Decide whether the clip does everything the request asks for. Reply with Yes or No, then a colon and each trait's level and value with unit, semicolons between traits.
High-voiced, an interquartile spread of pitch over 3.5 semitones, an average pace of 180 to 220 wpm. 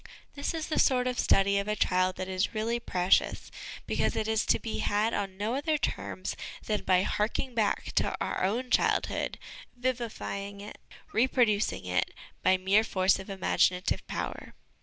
No: high, 210 Hz; average, 3.9 semitones; average, 165 wpm